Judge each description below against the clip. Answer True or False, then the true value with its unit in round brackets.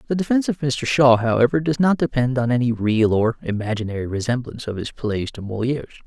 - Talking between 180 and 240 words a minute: True (200 wpm)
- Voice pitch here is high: False (125 Hz)